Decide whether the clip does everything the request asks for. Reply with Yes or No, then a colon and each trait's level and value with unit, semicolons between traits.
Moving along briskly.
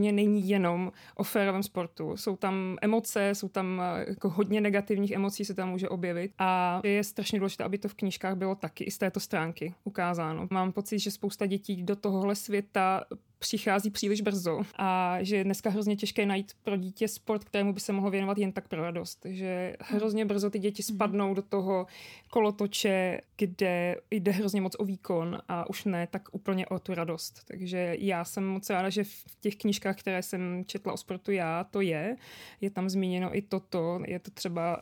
Yes: fast, 190 wpm